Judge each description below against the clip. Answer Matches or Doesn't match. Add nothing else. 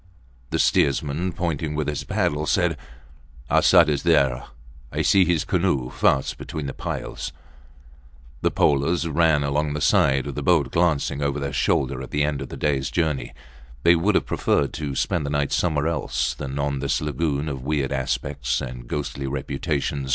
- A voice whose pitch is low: Matches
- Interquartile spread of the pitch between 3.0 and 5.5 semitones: Doesn't match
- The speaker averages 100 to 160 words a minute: Doesn't match